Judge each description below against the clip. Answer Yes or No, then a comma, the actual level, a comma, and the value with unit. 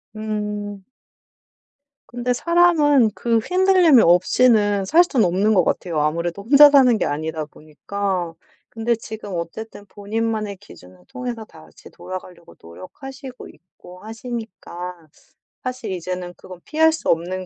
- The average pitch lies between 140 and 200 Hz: No, high, 210 Hz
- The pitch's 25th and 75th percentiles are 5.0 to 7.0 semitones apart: Yes, wide, 5.4 semitones